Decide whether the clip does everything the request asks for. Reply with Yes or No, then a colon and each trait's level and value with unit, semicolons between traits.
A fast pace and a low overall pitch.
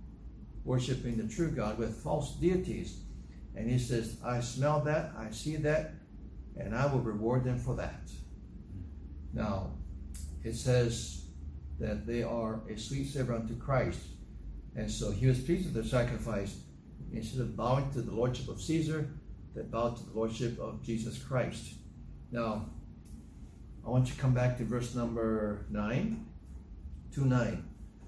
No: average, 150 wpm; low, 115 Hz